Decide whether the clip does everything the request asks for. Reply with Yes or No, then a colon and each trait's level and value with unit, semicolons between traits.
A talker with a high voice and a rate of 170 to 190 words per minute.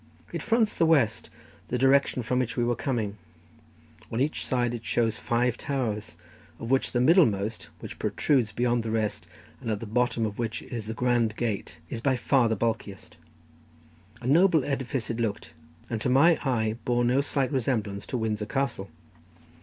No: low, 120 Hz; average, 175 wpm